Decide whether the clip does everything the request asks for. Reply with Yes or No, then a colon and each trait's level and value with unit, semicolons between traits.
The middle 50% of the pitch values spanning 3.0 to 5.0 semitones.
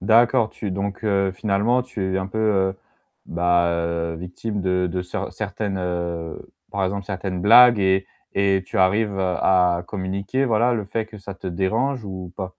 No: narrow, 2.6 semitones